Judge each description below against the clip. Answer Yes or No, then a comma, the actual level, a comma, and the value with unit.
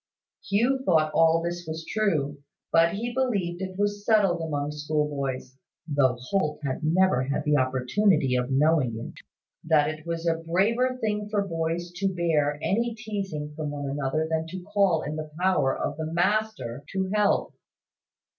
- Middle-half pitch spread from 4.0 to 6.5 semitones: Yes, average, 5.0 semitones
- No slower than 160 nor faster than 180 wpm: Yes, average, 165 wpm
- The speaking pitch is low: No, medium, 165 Hz